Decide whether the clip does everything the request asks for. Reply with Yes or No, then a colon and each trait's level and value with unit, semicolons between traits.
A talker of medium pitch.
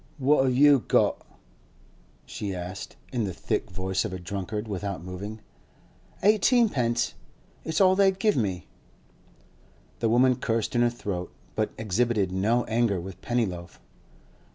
No: low, 110 Hz